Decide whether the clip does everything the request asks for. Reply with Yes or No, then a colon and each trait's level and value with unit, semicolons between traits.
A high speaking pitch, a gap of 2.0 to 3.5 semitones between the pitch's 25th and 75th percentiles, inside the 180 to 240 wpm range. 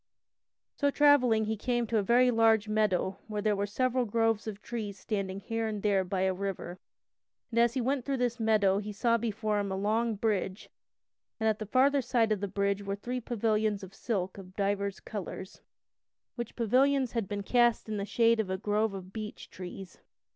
Yes: high, 215 Hz; average, 2.8 semitones; average, 200 wpm